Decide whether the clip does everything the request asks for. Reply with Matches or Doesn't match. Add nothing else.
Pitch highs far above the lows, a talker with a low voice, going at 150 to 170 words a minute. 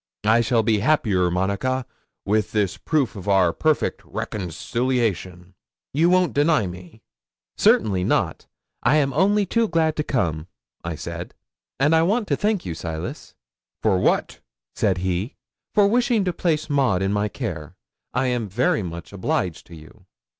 Matches